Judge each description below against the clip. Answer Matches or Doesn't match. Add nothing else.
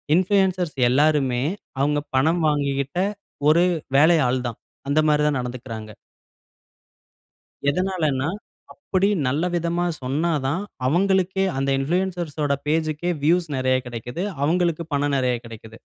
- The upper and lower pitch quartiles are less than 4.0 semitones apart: Doesn't match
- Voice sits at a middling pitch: Matches